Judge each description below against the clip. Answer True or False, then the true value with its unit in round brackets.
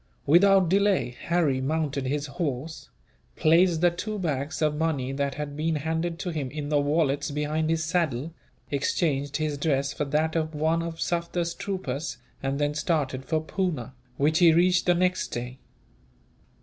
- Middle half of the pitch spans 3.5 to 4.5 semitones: False (3.0 semitones)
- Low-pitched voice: False (155 Hz)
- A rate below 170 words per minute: True (160 wpm)